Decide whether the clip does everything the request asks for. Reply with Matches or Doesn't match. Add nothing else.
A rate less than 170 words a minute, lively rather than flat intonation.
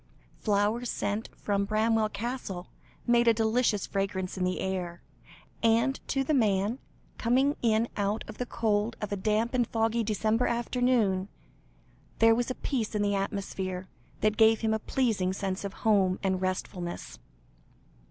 Doesn't match